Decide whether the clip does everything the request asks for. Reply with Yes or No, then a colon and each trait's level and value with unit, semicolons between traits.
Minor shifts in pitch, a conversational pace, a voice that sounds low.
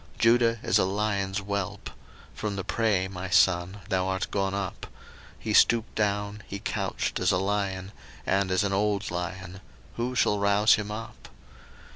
Yes: narrow, 1.8 semitones; average, 165 wpm; low, 100 Hz